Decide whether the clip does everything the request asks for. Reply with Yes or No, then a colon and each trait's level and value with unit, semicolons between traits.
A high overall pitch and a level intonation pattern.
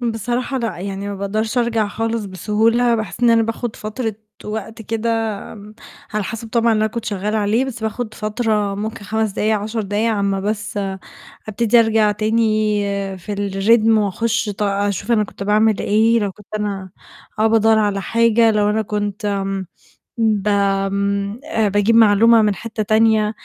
Yes: high, 215 Hz; narrow, 1.8 semitones